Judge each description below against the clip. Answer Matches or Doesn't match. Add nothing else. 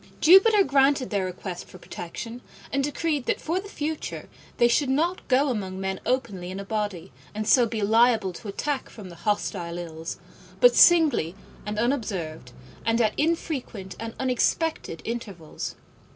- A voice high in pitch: Matches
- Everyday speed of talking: Matches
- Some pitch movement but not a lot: Doesn't match